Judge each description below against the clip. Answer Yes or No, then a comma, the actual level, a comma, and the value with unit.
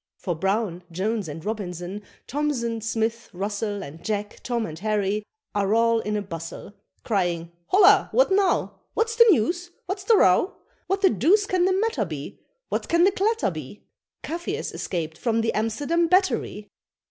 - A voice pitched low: No, high, 225 Hz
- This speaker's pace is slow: No, average, 160 wpm